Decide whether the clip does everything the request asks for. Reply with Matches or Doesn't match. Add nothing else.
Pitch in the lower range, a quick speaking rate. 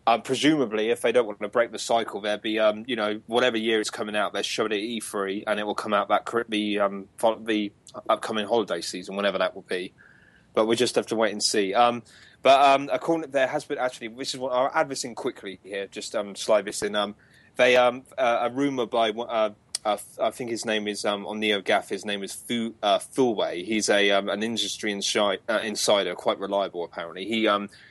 Matches